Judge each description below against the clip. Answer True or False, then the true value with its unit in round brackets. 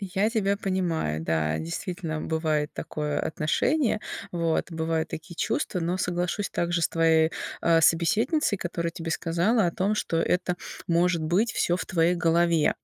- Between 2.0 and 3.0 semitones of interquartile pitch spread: True (2.4 semitones)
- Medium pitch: True (170 Hz)